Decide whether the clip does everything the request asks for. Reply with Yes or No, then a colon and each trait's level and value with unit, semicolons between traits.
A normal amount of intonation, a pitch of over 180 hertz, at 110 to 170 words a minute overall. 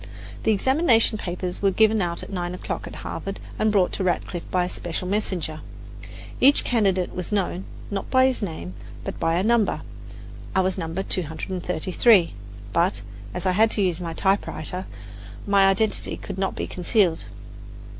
Yes: average, 3.0 semitones; high, 190 Hz; average, 165 wpm